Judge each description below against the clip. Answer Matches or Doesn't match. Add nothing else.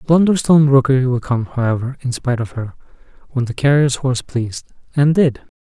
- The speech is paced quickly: Doesn't match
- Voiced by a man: Matches